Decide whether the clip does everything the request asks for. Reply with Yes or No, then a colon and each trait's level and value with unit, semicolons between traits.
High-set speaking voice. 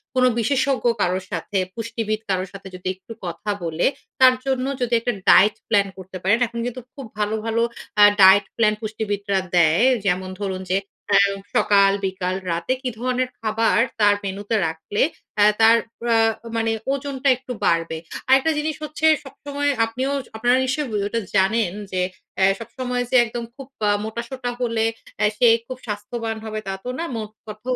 Yes: high, 220 Hz